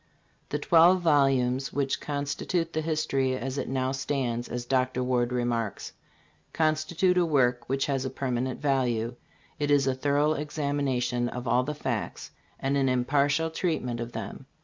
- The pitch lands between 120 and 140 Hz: Yes, low, 135 Hz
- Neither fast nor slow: Yes, average, 160 wpm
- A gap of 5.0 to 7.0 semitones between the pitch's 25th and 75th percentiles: No, average, 2.9 semitones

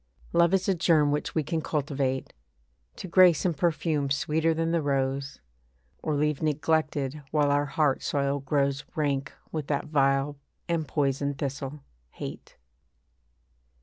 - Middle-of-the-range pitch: Yes, medium, 145 Hz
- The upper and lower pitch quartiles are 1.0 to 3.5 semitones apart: Yes, narrow, 2.4 semitones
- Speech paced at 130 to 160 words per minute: Yes, average, 140 wpm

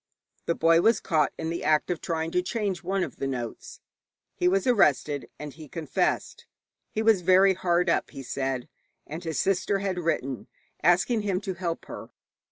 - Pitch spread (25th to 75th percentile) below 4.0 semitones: Yes, average, 3.6 semitones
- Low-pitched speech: No, medium, 175 Hz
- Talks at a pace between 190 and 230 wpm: No, average, 180 wpm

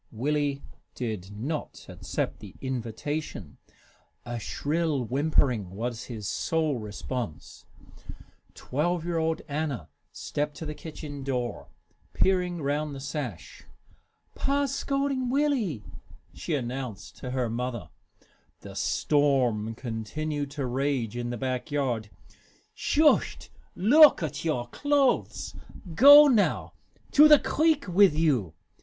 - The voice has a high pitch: No, medium, 145 Hz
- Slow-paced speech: Yes, slow, 115 wpm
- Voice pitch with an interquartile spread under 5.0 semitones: No, wide, 5.6 semitones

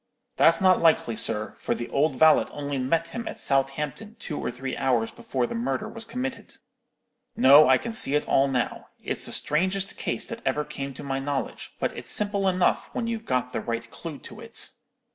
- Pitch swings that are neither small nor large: No, wide, 6.8 semitones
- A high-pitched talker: No, medium, 145 Hz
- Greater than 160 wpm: Yes, average, 200 wpm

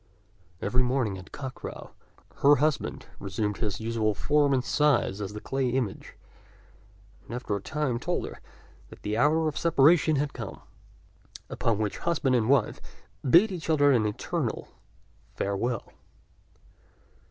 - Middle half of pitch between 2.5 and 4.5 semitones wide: No, wide, 5.4 semitones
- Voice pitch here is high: No, low, 125 Hz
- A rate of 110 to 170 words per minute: Yes, average, 145 wpm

